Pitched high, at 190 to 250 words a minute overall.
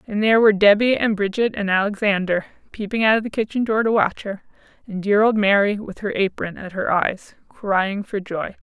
Yes: high, 205 Hz; fast, 205 wpm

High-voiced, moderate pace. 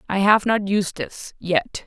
Yes: high, 195 Hz; average, 160 wpm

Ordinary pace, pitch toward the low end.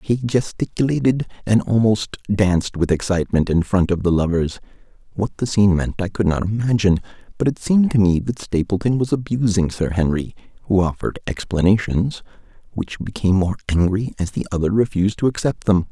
Yes: average, 170 wpm; low, 100 Hz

